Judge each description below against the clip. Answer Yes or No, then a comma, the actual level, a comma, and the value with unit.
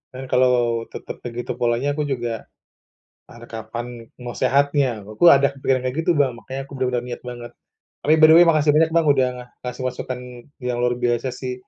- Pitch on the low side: Yes, low, 130 Hz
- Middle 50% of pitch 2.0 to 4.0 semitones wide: Yes, narrow, 2.5 semitones